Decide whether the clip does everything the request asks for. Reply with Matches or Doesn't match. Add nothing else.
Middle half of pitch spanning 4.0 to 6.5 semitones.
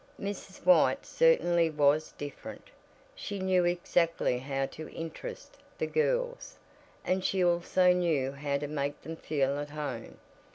Matches